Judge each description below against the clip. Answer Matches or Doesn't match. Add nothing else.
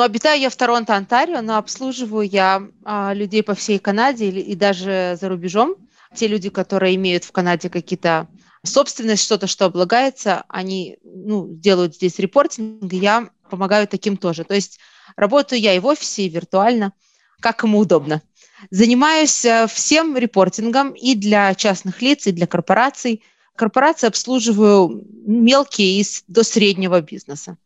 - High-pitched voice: Matches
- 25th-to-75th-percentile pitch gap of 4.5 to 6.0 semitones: Doesn't match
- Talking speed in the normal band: Matches